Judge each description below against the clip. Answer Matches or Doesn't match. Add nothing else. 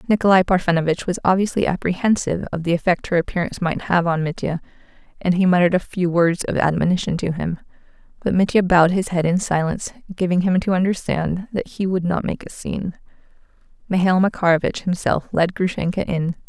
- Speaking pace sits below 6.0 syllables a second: Doesn't match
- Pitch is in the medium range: Matches